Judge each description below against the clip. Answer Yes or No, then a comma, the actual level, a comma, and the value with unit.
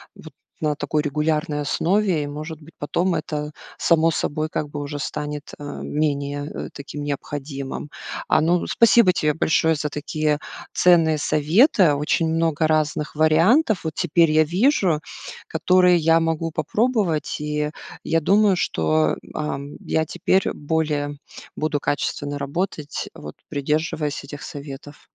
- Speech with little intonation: Yes, narrow, 2.2 semitones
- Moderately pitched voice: Yes, medium, 155 Hz